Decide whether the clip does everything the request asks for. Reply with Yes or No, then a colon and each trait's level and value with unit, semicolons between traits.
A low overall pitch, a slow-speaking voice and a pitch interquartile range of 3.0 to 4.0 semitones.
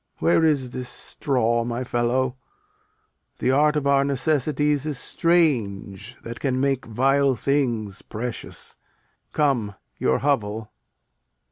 Yes: low, 130 Hz; slow, 115 wpm; average, 3.5 semitones